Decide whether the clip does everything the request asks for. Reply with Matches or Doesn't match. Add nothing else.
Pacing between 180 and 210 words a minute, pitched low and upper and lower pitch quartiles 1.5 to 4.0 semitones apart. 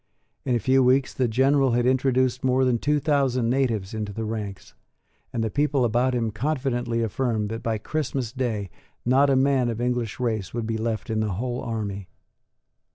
Matches